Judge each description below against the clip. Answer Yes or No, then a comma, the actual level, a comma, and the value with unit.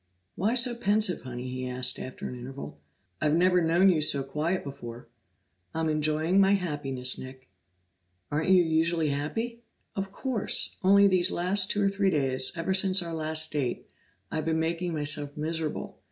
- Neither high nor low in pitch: Yes, medium, 160 Hz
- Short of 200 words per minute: Yes, average, 165 wpm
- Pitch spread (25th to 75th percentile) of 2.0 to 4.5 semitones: No, average, 4.9 semitones